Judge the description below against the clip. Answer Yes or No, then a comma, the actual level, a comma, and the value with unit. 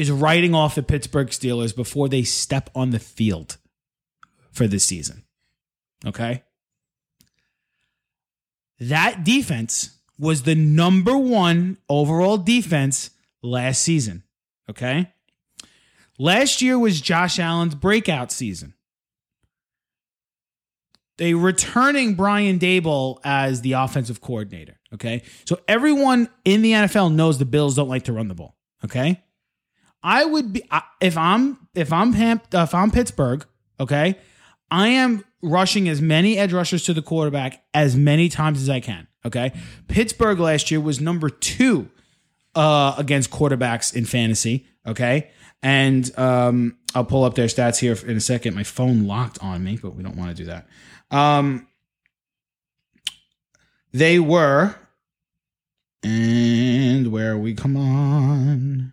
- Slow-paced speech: Yes, slow, 130 wpm